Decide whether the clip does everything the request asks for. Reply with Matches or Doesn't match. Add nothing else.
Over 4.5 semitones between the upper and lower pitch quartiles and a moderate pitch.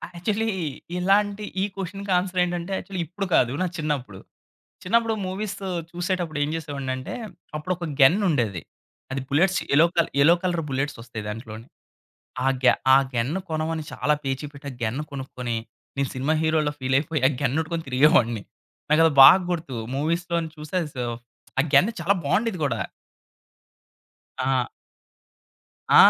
Matches